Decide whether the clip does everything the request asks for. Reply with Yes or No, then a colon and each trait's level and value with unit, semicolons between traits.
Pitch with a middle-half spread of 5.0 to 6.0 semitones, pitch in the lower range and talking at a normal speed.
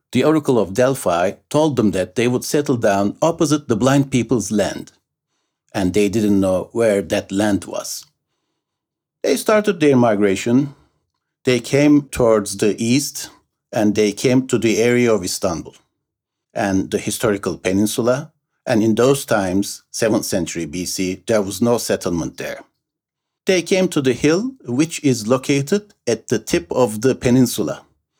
Yes: wide, 5.4 semitones; low, 120 Hz; average, 150 wpm